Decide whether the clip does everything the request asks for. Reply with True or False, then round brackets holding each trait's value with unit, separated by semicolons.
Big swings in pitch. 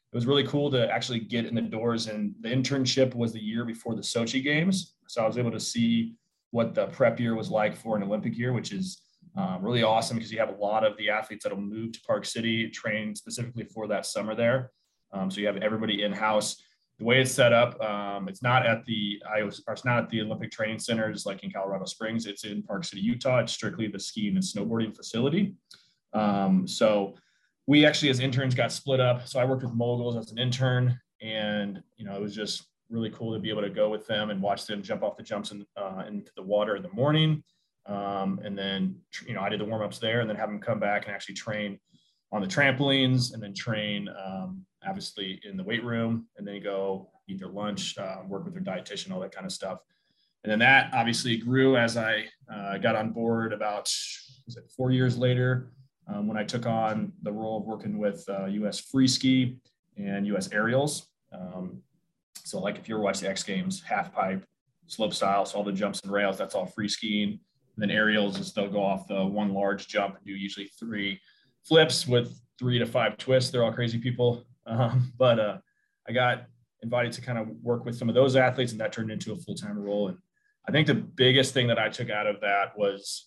False (3.7 semitones)